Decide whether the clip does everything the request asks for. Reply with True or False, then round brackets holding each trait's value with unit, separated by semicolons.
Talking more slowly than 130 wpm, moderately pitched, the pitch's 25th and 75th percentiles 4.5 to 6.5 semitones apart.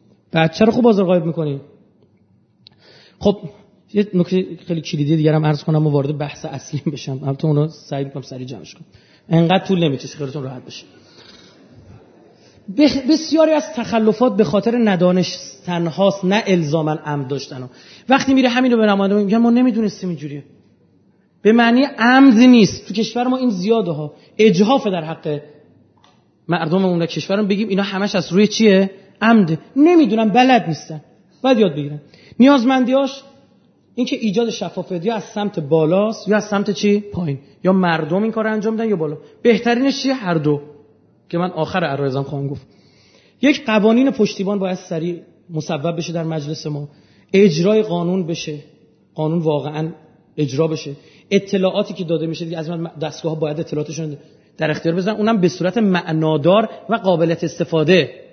False (155 wpm; 180 Hz; 5.6 semitones)